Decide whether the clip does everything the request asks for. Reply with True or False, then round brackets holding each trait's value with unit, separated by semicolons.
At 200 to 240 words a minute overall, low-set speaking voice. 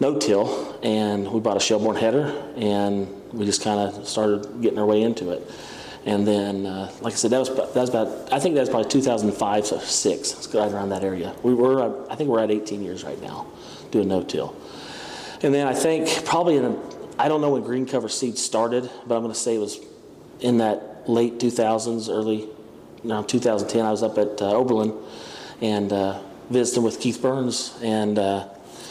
True (205 wpm; 110 Hz)